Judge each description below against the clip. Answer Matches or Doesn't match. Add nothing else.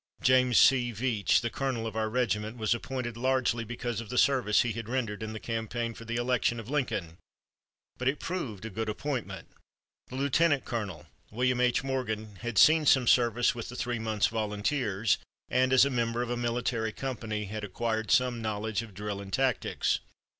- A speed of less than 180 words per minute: Doesn't match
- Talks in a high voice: Doesn't match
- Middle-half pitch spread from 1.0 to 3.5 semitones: Matches